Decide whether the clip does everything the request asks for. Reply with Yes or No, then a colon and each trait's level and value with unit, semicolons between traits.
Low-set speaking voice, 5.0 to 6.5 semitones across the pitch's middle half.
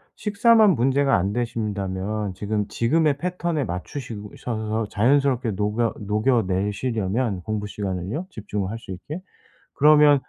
Yes: low, 115 Hz; wide, 5.6 semitones